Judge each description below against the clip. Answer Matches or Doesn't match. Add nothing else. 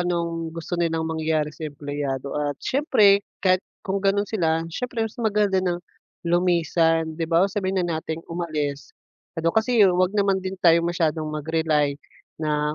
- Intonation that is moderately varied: Matches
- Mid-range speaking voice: Matches